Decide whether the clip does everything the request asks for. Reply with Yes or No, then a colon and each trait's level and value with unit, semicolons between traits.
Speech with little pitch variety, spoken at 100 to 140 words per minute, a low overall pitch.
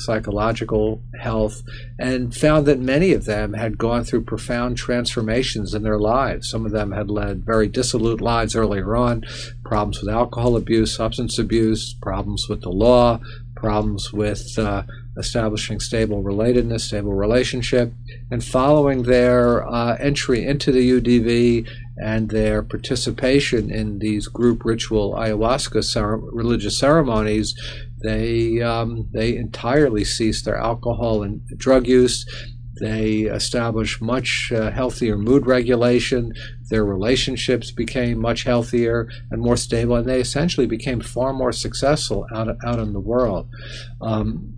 Yes: narrow, 1.9 semitones; slow, 135 wpm; low, 115 Hz